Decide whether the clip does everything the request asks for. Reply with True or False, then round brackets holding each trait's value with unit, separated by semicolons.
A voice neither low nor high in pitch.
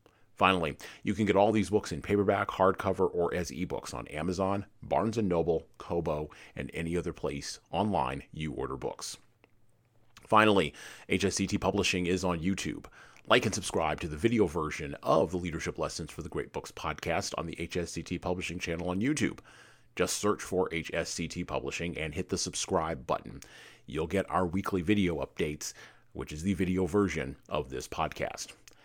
False (90 Hz)